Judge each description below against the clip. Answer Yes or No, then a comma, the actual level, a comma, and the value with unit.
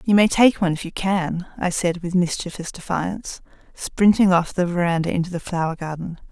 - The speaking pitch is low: No, medium, 175 Hz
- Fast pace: No, average, 190 wpm